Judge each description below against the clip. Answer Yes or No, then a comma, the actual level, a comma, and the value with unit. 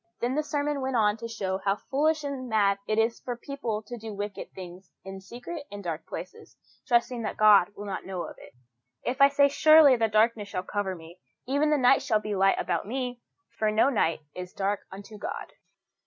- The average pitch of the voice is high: Yes, high, 220 Hz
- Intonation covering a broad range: No, average, 4.8 semitones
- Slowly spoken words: No, fast, 205 wpm